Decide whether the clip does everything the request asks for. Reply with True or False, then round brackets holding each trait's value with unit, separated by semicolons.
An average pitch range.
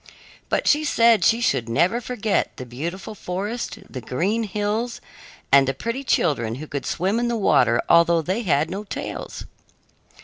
False (8.0 semitones)